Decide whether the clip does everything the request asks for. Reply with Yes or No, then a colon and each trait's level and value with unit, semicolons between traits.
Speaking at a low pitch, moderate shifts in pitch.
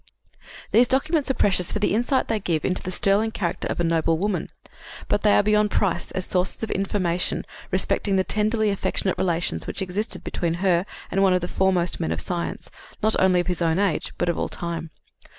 No: high, 190 Hz; average, 3.3 semitones